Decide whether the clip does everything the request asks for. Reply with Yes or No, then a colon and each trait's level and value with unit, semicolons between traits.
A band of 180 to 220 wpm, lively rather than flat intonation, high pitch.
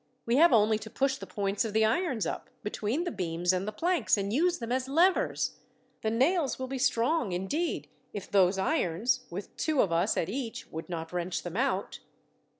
Yes: average, 200 wpm; wide, 6.2 semitones; high, 220 Hz